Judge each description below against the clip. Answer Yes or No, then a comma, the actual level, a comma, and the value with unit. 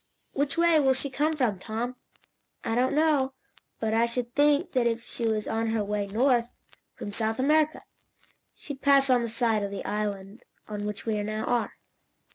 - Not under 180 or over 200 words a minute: Yes, average, 185 wpm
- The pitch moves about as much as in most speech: Yes, average, 4.2 semitones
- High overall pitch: Yes, high, 235 Hz